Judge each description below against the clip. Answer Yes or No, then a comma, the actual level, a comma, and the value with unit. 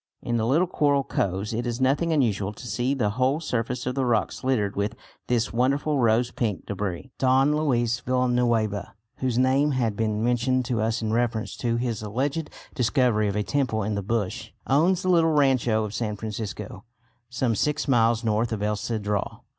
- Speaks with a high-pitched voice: No, low, 120 Hz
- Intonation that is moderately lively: Yes, average, 3.4 semitones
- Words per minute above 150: Yes, average, 185 wpm